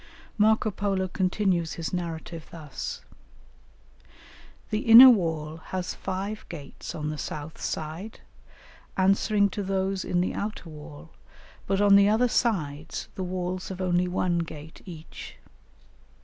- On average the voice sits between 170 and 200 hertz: Yes, medium, 185 Hz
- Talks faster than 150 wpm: No, slow, 135 wpm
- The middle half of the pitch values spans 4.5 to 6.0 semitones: No, average, 3.6 semitones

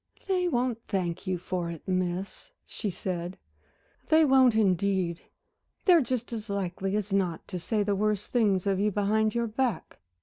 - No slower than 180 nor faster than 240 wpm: No, average, 165 wpm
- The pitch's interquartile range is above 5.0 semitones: No, average, 3.8 semitones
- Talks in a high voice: Yes, high, 200 Hz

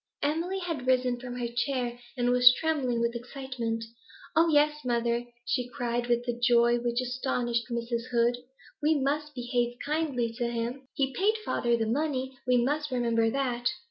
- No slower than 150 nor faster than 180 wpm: Yes, average, 165 wpm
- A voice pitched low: No, high, 245 Hz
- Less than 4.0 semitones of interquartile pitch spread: Yes, narrow, 2.5 semitones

